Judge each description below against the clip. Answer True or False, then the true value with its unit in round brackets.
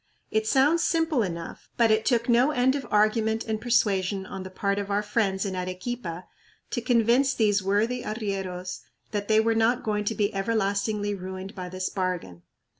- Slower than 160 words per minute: False (180 wpm)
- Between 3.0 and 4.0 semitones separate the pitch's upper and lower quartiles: True (3.4 semitones)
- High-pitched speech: True (210 Hz)